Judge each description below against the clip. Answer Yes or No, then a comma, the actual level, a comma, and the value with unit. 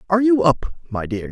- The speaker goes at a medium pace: No, fast, 230 wpm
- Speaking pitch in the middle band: Yes, medium, 170 Hz